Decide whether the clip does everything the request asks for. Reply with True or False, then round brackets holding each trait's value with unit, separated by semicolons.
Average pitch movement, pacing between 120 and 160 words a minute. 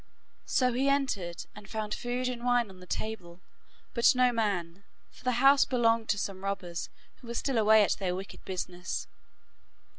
False (4.5 semitones; 175 wpm)